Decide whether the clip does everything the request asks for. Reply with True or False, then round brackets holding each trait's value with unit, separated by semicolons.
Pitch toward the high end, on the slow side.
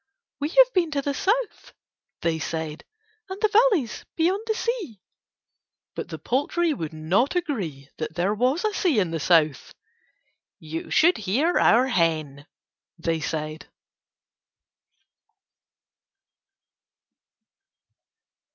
True (235 Hz; 115 wpm)